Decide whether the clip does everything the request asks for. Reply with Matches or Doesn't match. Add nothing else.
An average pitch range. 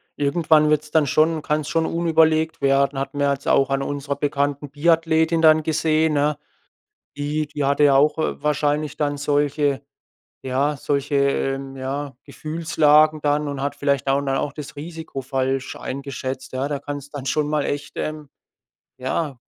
Doesn't match